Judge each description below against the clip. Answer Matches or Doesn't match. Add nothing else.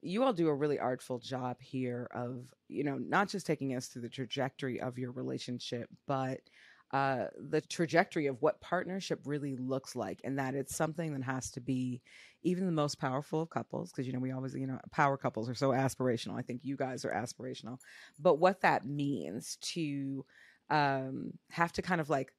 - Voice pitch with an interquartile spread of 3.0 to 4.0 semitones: Matches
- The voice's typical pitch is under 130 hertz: Doesn't match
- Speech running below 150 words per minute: Doesn't match